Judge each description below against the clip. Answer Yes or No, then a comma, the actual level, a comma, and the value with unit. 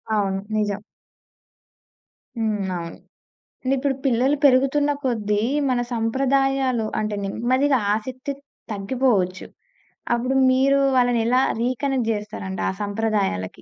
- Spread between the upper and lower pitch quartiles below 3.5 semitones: No, average, 4.1 semitones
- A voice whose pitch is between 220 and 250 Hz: Yes, high, 240 Hz